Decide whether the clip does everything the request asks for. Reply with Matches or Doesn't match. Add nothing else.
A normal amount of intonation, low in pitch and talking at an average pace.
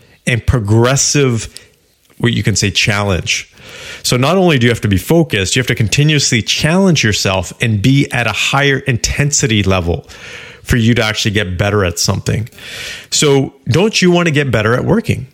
Matches